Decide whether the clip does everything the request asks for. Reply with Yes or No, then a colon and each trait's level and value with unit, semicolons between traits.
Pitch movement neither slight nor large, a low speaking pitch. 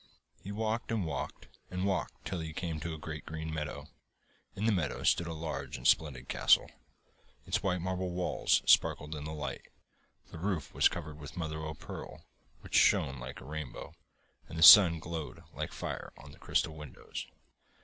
Yes: average, 3.0 semitones; very low, 80 Hz